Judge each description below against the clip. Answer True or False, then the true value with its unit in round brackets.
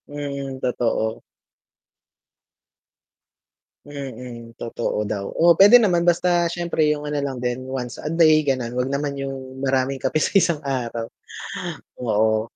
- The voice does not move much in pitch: False (3.9 semitones)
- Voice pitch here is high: False (135 Hz)